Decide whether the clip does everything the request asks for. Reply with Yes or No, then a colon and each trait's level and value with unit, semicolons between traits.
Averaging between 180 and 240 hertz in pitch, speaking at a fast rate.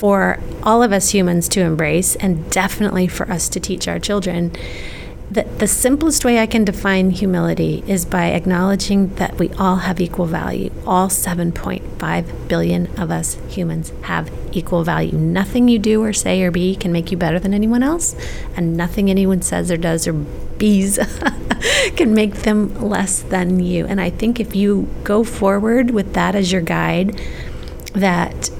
No: medium, 185 Hz; average, 170 wpm